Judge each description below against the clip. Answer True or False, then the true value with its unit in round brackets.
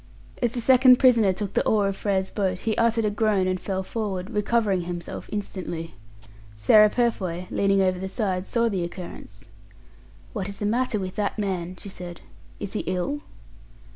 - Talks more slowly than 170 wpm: False (175 wpm)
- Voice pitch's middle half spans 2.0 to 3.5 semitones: True (2.9 semitones)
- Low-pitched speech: False (200 Hz)